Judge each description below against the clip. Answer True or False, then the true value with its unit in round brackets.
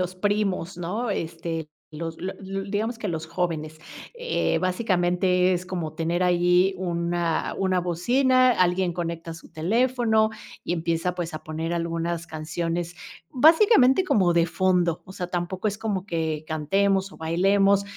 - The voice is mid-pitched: True (180 Hz)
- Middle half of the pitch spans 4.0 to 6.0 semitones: False (2.9 semitones)